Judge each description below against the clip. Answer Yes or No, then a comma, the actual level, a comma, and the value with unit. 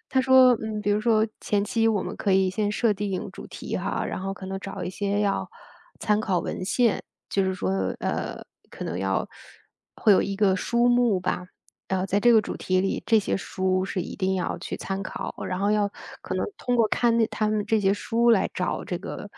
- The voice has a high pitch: Yes, high, 205 Hz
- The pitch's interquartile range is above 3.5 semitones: No, average, 2.7 semitones